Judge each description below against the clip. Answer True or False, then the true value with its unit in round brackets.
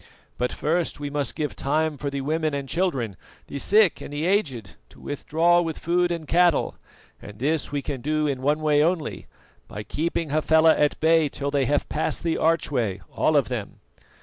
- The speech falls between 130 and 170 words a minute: False (190 wpm)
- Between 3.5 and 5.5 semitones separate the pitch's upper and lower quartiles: False (2.7 semitones)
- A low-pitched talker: False (150 Hz)